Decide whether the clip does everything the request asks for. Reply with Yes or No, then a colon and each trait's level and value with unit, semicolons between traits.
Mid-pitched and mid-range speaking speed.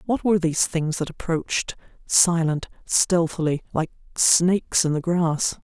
No: medium, 170 Hz; slow, 125 wpm